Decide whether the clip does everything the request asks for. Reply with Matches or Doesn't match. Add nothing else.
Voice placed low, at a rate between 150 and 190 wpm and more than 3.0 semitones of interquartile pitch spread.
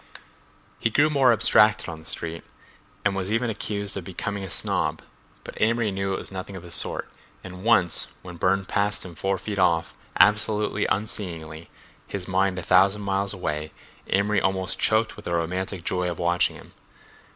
Doesn't match